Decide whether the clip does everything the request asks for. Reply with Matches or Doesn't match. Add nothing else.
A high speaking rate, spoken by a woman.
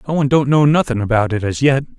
Doesn't match